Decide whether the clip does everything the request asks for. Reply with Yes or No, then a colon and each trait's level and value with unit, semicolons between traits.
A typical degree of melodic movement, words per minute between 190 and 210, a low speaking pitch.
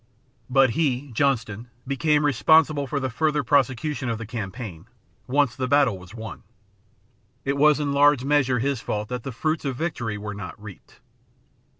No: average, 4.3 semitones; average, 165 wpm; low, 130 Hz